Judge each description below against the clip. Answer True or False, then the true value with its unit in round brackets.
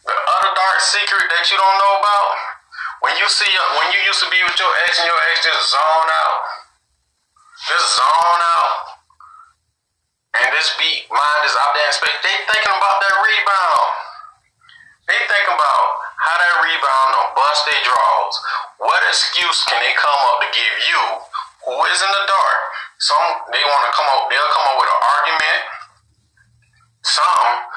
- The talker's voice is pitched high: True (200 Hz)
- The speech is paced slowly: False (175 wpm)